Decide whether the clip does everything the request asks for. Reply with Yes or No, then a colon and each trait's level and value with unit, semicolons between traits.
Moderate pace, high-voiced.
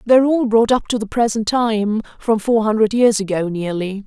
Yes: average, 190 wpm; high, 220 Hz